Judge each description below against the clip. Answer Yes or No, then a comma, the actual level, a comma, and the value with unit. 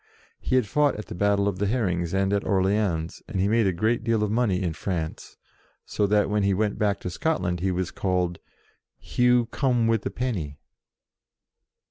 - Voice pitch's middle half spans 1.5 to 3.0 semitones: No, average, 3.6 semitones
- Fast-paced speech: No, average, 190 wpm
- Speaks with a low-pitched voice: Yes, low, 100 Hz